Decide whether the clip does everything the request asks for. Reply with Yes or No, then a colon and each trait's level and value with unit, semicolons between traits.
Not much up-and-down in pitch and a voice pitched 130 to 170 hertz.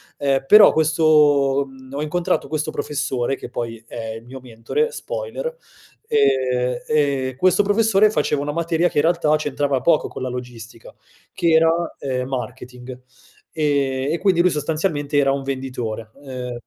No: average, 4.0 semitones; medium, 140 Hz